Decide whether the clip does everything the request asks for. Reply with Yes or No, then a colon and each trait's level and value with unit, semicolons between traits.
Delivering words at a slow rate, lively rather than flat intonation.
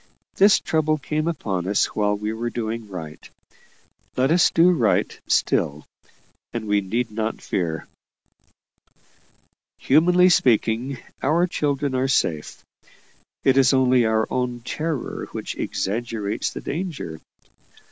Yes: slow, 120 wpm; wide, 6.0 semitones